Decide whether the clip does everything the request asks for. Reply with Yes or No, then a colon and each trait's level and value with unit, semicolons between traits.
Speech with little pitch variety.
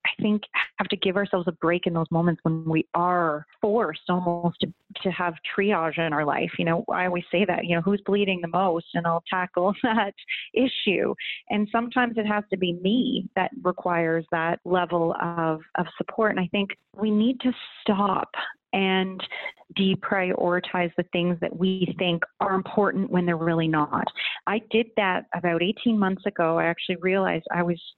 No: average, 3.0 semitones